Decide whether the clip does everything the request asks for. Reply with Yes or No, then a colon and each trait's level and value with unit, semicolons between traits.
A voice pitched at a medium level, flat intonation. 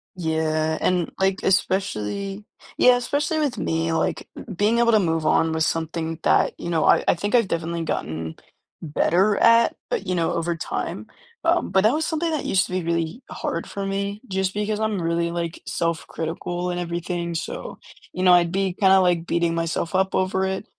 No: medium, 180 Hz; average, 3.1 semitones